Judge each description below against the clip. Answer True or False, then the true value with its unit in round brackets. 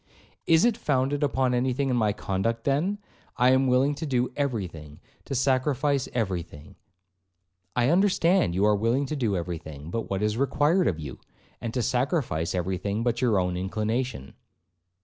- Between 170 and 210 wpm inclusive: False (160 wpm)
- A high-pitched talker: False (120 Hz)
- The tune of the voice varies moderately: False (6.7 semitones)